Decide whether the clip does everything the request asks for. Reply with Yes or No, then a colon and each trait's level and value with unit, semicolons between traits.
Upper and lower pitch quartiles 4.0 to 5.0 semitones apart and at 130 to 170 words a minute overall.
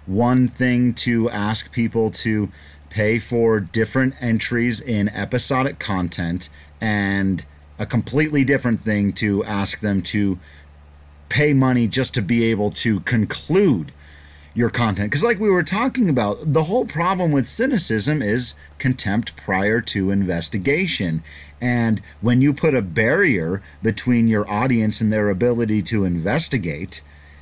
Yes: average, 4.5 semitones; slow, 135 wpm